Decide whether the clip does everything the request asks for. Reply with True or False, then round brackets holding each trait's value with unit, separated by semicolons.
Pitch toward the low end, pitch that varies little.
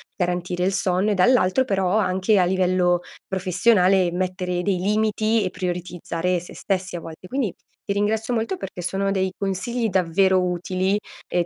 False (185 Hz; 2.1 semitones)